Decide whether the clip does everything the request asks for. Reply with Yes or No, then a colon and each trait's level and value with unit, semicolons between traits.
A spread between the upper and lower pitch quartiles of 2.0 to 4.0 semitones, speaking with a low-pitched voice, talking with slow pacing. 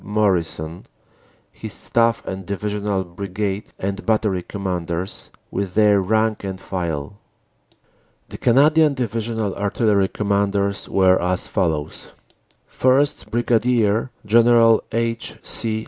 Yes: average, 3.2 semitones; low, 100 Hz; slow, 100 wpm